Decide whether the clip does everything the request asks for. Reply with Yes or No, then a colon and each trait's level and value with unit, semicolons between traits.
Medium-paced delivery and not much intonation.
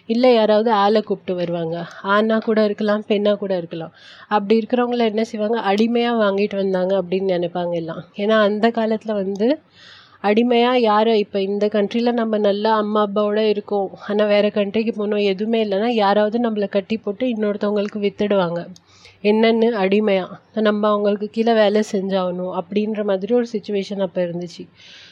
No: fast, 145 wpm; narrow, 1.9 semitones